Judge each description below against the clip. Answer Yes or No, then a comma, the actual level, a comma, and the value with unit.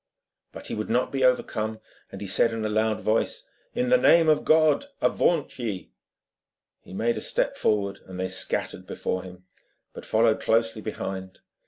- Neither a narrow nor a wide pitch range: Yes, average, 4.5 semitones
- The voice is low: Yes, low, 110 Hz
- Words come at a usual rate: Yes, average, 170 wpm